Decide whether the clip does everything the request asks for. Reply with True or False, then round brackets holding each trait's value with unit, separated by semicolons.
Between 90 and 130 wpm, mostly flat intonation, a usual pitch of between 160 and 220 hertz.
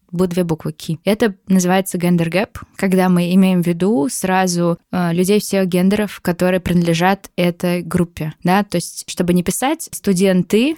False (155 wpm; 1.8 semitones; 185 Hz)